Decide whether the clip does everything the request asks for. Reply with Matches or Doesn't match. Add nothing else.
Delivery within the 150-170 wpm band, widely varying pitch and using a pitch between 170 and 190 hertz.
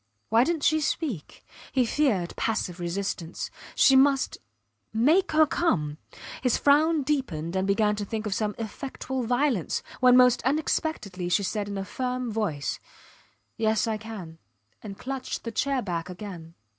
Doesn't match